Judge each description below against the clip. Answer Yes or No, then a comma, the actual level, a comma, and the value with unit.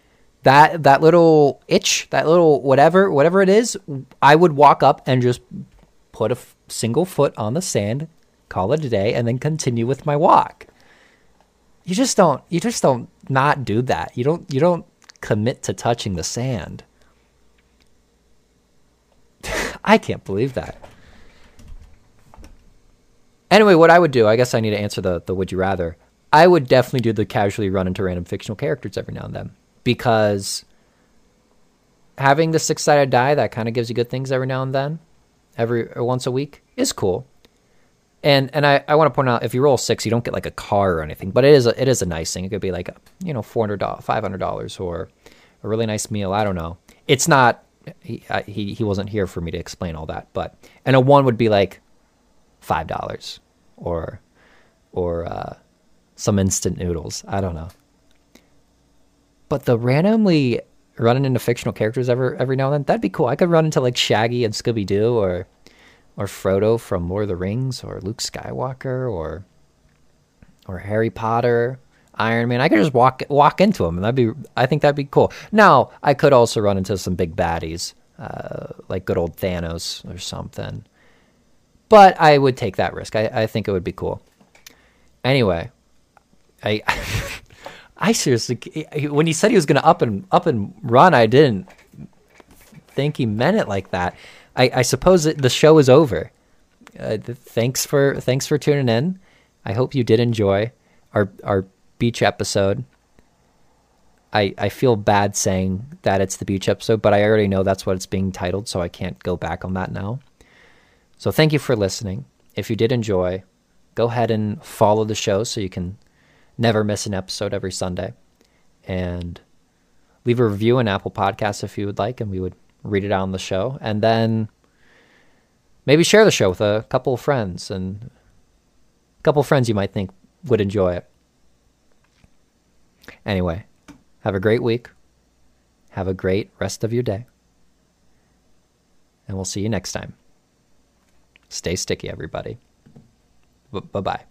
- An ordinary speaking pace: Yes, average, 185 wpm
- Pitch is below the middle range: Yes, low, 115 Hz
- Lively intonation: Yes, wide, 5.9 semitones